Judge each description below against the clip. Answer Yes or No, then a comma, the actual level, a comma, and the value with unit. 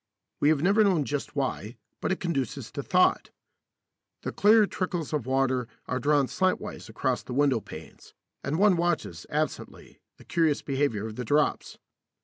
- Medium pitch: Yes, medium, 145 Hz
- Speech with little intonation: No, average, 4.9 semitones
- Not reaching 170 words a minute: Yes, average, 160 wpm